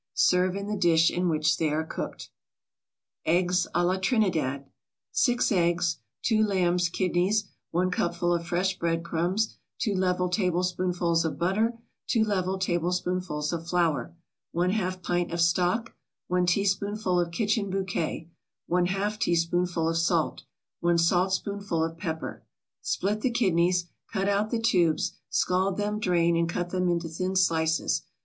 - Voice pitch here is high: No, medium, 180 Hz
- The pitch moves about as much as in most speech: No, narrow, 2.3 semitones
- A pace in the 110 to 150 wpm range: Yes, average, 140 wpm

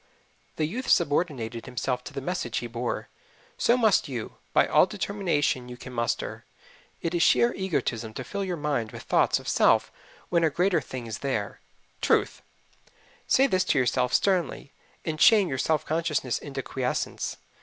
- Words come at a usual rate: Yes, average, 170 wpm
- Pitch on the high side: No, medium, 145 Hz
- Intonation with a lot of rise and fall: Yes, wide, 6.4 semitones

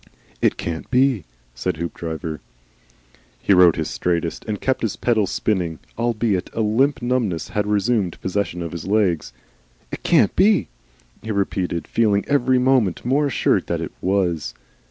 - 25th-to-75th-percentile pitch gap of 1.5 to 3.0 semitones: No, wide, 5.6 semitones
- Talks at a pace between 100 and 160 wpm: Yes, average, 150 wpm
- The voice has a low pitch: Yes, low, 100 Hz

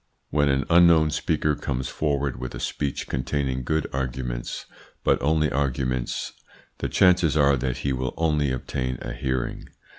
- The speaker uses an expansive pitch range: No, average, 3.0 semitones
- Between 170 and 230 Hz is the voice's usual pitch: No, very low, 70 Hz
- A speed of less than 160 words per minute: Yes, average, 150 wpm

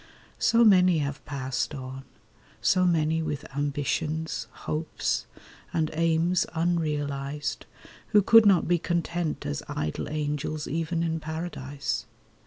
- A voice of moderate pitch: Yes, medium, 155 Hz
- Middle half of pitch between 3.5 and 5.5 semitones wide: No, average, 2.9 semitones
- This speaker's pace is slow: Yes, slow, 115 wpm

